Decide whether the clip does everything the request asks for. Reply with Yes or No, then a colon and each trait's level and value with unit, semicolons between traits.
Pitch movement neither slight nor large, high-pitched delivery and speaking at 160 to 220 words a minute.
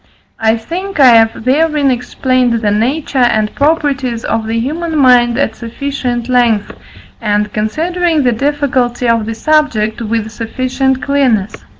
No: average, 3.9 semitones; high, 245 Hz; slow, 135 wpm